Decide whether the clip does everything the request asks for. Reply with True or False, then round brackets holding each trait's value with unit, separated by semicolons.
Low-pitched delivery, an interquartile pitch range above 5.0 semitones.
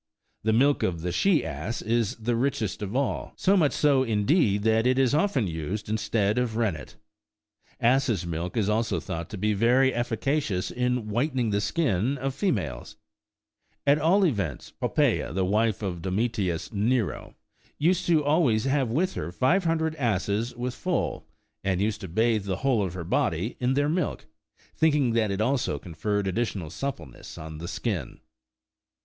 True (115 Hz; 5.6 semitones)